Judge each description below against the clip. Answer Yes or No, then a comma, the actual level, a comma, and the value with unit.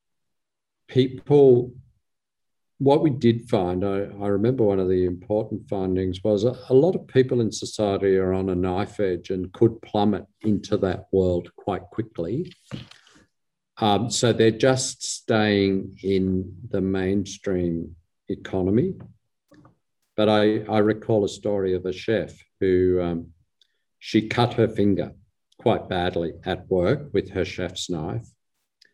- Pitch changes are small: No, average, 3.3 semitones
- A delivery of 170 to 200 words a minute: No, slow, 135 wpm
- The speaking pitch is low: Yes, low, 100 Hz